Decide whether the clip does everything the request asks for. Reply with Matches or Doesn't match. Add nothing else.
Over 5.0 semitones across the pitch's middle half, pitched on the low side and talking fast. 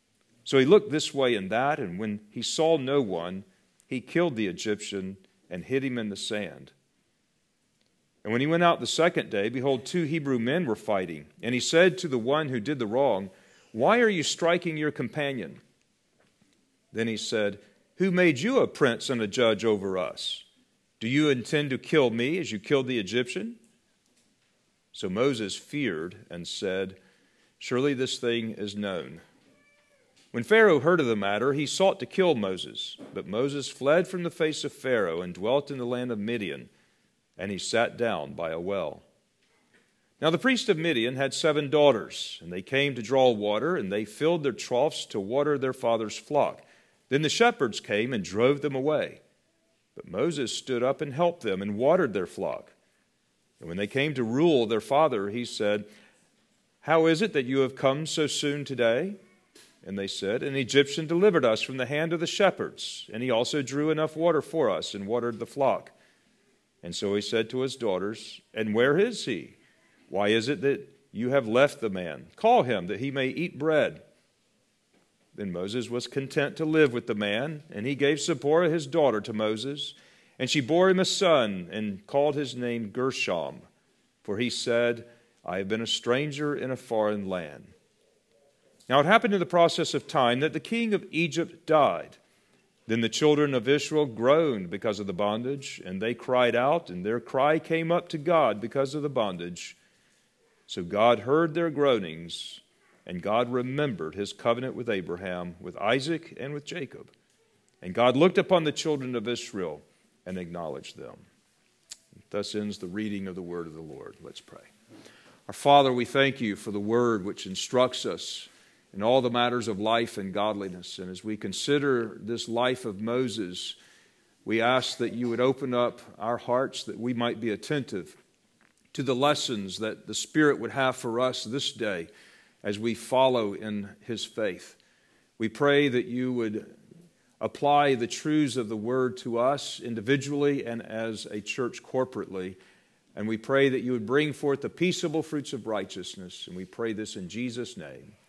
Doesn't match